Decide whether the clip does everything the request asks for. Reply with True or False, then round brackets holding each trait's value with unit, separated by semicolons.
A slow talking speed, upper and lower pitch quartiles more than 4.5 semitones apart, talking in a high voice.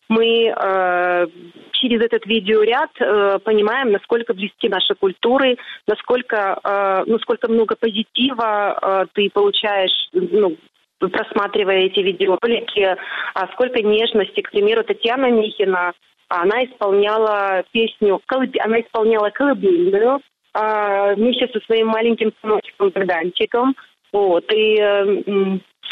False (105 wpm; 2.8 semitones; 215 Hz)